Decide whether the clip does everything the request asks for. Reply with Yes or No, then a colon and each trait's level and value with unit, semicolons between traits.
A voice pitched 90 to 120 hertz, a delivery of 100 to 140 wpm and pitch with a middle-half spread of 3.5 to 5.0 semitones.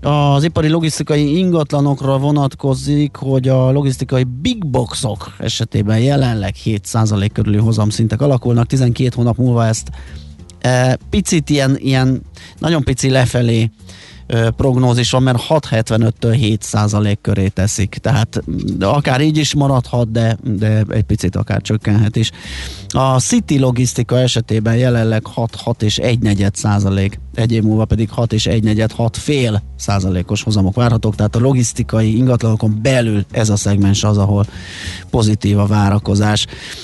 Yes: low, 115 Hz; average, 135 wpm; average, 3.8 semitones